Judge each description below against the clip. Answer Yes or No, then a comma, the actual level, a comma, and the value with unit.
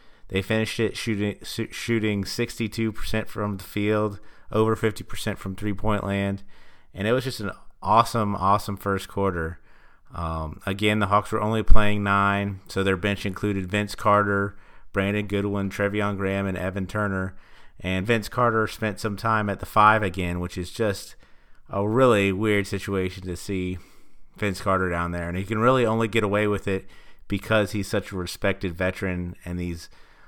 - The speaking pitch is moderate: No, low, 100 Hz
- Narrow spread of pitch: Yes, narrow, 2.0 semitones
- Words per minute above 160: Yes, average, 175 wpm